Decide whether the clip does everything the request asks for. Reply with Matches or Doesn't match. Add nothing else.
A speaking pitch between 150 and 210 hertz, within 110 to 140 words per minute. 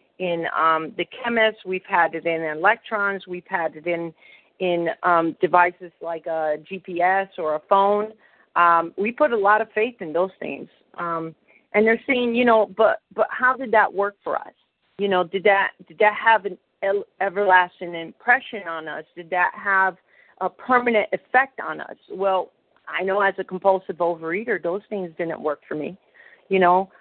Doesn't match